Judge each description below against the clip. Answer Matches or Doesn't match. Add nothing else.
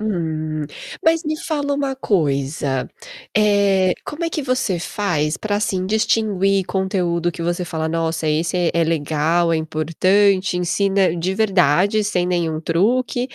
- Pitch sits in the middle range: Matches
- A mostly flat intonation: Doesn't match